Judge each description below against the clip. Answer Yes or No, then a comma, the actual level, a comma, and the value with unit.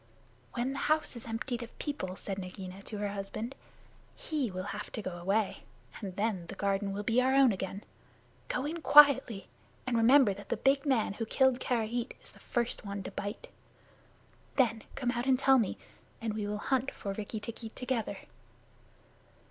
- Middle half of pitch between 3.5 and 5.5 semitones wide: Yes, average, 4.4 semitones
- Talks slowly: No, average, 180 wpm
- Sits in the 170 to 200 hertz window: No, high, 225 Hz